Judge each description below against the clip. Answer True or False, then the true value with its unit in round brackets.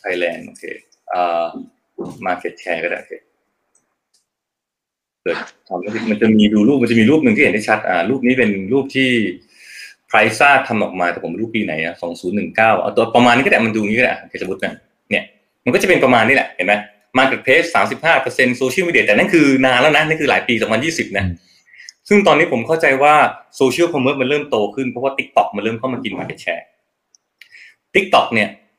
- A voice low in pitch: True (115 Hz)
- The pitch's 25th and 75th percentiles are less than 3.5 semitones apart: False (4.7 semitones)